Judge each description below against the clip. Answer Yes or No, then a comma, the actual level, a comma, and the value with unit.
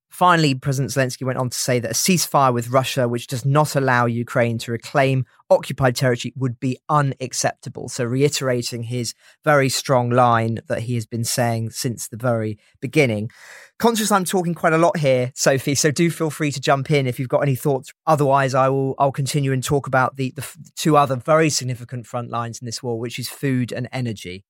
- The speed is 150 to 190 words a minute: No, fast, 205 wpm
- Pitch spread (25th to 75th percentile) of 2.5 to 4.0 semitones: Yes, average, 3.0 semitones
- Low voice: Yes, low, 130 Hz